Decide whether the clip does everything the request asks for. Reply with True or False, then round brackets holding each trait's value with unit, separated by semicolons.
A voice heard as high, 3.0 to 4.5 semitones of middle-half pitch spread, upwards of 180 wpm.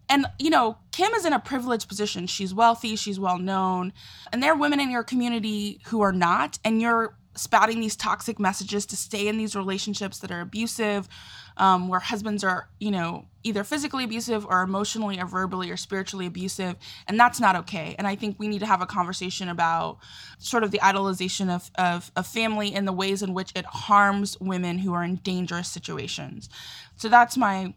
True (200 Hz; 3.3 semitones; 200 wpm)